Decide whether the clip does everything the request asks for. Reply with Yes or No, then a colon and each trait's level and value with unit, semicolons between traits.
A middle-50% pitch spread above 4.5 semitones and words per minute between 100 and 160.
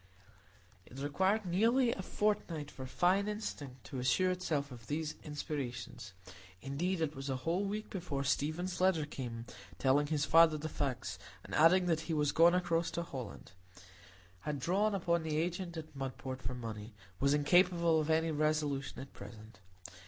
Yes: average, 5.0 semitones; average, 155 wpm